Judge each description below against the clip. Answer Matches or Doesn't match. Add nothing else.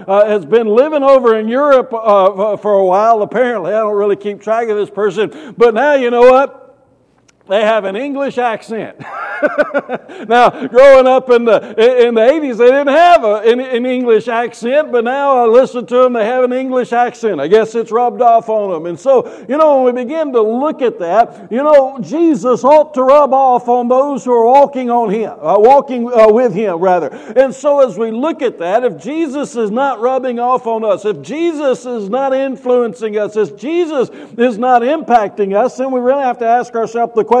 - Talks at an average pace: Doesn't match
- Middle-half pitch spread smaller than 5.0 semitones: Matches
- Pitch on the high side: Matches